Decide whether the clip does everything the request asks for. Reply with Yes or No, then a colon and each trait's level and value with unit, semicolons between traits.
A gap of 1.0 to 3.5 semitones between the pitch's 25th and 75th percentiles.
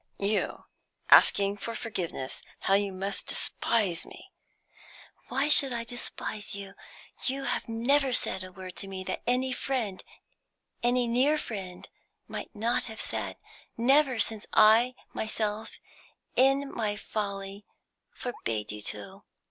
No: average, 4.1 semitones